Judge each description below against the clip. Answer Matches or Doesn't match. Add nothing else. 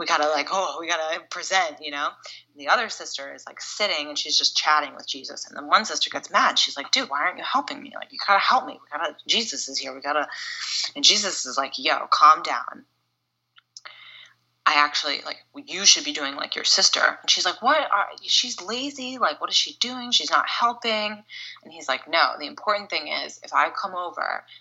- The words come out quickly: Matches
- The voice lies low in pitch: Doesn't match